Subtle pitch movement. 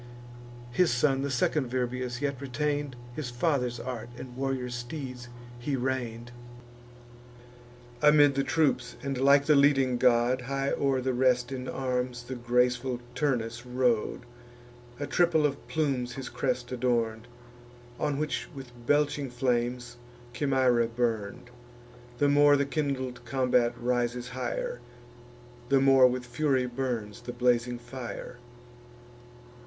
Yes: narrow, 2.0 semitones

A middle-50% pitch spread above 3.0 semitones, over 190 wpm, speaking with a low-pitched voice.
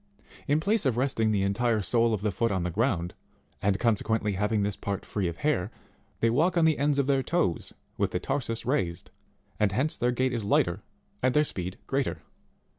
Yes: average, 5.3 semitones; average, 200 wpm; low, 115 Hz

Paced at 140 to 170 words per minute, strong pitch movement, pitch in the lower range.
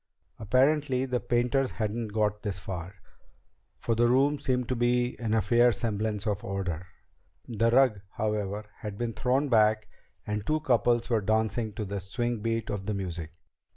No: average, 165 wpm; average, 2.8 semitones; low, 110 Hz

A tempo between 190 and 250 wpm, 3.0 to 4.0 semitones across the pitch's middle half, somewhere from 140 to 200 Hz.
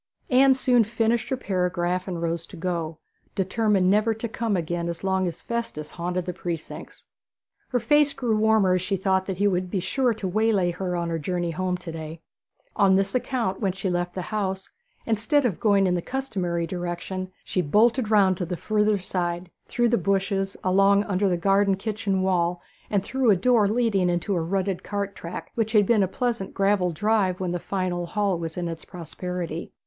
Yes: average, 200 wpm; average, 3.3 semitones; high, 190 Hz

